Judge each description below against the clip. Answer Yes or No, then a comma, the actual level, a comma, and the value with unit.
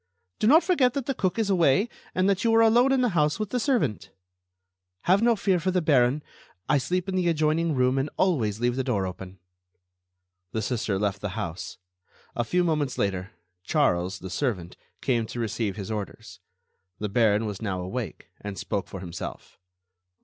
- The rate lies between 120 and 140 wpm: No, average, 185 wpm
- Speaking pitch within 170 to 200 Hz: No, low, 130 Hz